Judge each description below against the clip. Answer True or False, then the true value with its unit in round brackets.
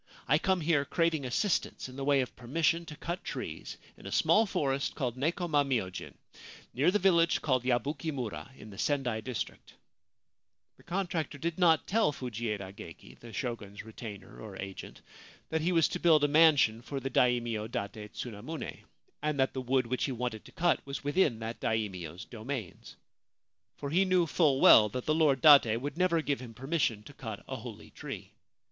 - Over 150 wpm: True (180 wpm)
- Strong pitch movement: True (5.9 semitones)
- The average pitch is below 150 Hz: True (135 Hz)